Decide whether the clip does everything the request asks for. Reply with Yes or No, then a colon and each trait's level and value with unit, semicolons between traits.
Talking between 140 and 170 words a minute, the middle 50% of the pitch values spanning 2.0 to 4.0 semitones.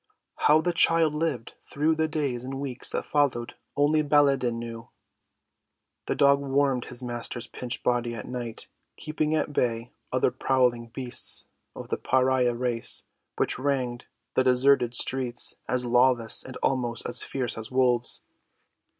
Yes: average, 145 wpm; average, 2.7 semitones